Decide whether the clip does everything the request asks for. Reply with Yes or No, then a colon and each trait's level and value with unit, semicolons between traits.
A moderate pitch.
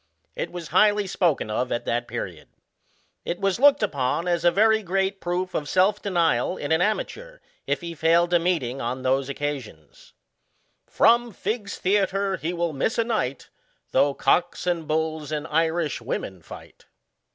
Yes: medium, 170 Hz